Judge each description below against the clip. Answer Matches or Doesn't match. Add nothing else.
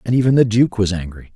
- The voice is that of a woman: Doesn't match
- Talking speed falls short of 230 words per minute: Doesn't match